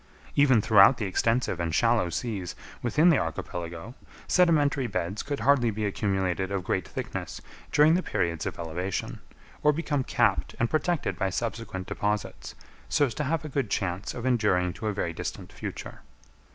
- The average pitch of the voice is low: Yes, low, 110 Hz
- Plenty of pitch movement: Yes, wide, 6.9 semitones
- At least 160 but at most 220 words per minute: Yes, average, 165 wpm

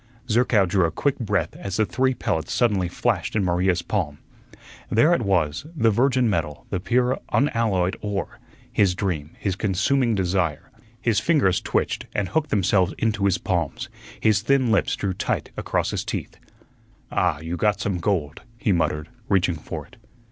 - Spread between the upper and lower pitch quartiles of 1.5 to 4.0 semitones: No, average, 4.4 semitones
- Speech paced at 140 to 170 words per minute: Yes, average, 165 wpm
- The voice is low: Yes, low, 100 Hz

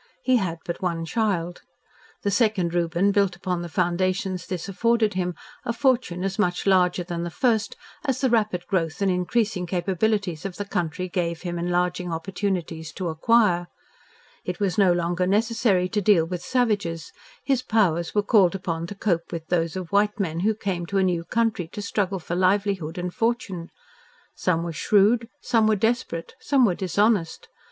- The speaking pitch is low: No, medium, 185 Hz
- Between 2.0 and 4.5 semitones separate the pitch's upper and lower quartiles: Yes, average, 3.4 semitones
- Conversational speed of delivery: Yes, average, 175 wpm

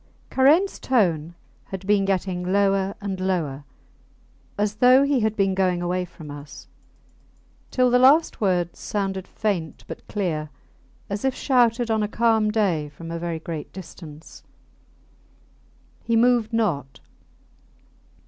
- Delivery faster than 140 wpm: No, slow, 135 wpm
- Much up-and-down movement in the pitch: No, average, 4.6 semitones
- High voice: Yes, high, 195 Hz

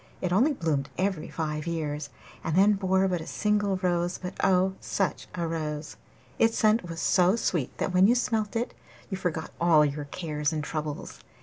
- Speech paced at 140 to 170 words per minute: No, average, 185 wpm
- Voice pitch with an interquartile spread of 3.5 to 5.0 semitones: Yes, average, 3.9 semitones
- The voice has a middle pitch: Yes, medium, 175 Hz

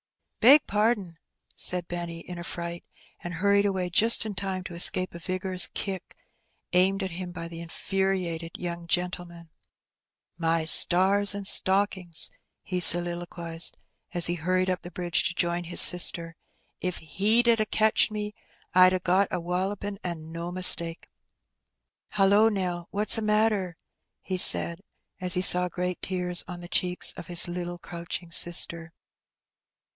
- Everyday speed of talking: Yes, average, 155 wpm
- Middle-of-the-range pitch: Yes, medium, 180 Hz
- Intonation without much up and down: Yes, narrow, 2.0 semitones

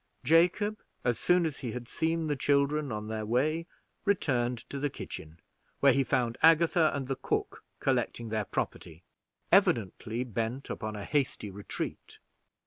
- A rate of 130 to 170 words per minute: Yes, average, 150 wpm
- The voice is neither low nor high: No, low, 130 Hz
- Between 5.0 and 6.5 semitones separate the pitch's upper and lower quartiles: Yes, wide, 5.6 semitones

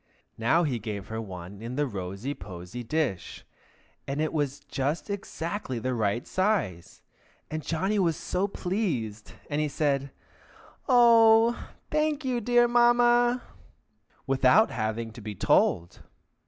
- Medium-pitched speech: Yes, medium, 145 Hz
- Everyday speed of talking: No, slow, 125 wpm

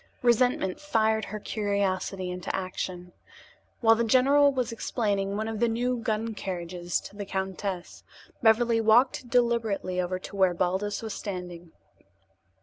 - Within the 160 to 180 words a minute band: No, average, 140 wpm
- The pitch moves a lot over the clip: No, average, 3.7 semitones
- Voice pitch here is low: No, high, 210 Hz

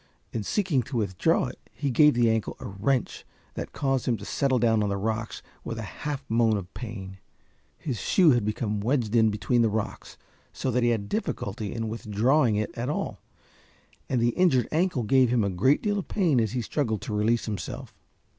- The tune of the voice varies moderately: Yes, average, 3.8 semitones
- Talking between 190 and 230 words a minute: Yes, average, 200 wpm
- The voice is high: No, low, 115 Hz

